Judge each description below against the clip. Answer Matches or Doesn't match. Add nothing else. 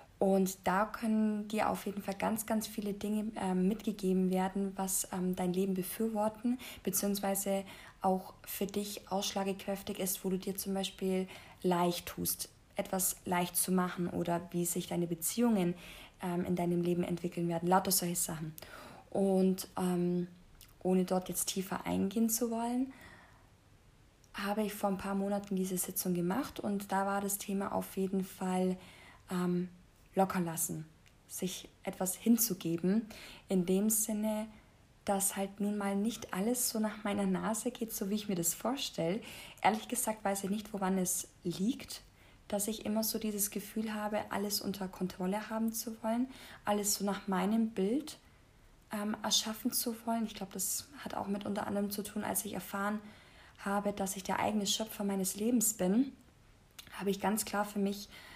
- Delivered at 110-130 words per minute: Doesn't match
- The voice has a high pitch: Matches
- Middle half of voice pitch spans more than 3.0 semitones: Doesn't match